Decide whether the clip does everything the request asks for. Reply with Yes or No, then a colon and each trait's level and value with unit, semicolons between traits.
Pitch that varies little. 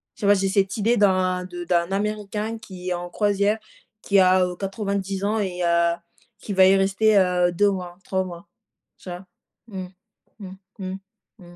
Yes: narrow, 2.0 semitones